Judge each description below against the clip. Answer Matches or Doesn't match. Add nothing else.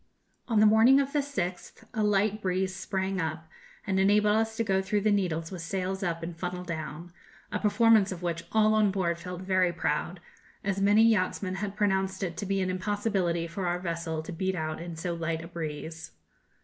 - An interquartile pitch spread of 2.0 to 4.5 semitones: Matches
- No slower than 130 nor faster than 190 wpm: Doesn't match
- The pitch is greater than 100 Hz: Matches